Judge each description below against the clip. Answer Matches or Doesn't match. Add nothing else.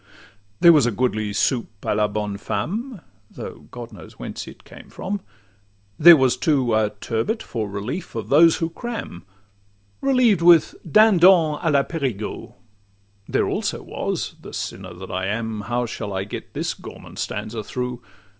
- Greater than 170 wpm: Doesn't match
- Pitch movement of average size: Doesn't match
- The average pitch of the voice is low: Matches